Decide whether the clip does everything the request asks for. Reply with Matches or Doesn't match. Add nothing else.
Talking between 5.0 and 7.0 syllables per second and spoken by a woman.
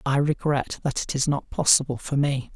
Doesn't match